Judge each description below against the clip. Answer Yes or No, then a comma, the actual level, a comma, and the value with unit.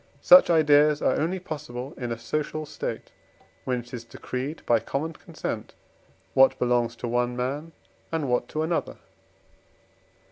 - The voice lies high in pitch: No, low, 135 Hz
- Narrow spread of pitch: No, average, 4.1 semitones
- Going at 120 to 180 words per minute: Yes, average, 145 wpm